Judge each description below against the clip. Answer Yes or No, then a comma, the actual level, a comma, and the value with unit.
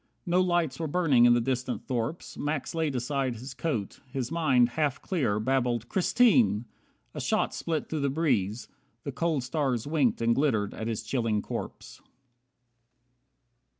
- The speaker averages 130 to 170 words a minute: Yes, average, 150 wpm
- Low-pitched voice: Yes, low, 130 Hz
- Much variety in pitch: No, average, 4.9 semitones